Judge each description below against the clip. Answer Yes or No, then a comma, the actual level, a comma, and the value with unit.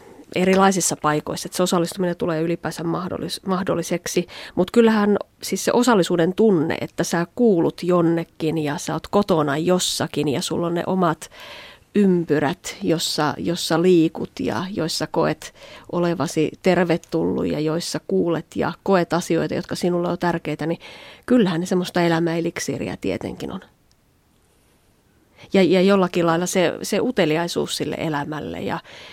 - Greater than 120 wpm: Yes, average, 130 wpm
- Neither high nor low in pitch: Yes, medium, 170 Hz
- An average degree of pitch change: No, narrow, 2.2 semitones